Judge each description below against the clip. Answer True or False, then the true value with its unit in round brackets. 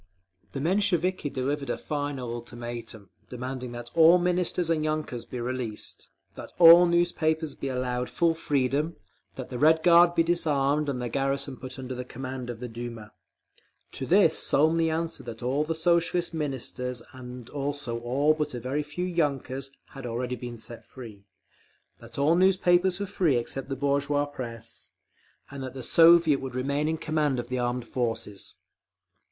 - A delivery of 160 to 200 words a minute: True (165 wpm)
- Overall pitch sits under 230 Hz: True (135 Hz)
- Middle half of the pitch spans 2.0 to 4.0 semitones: False (4.5 semitones)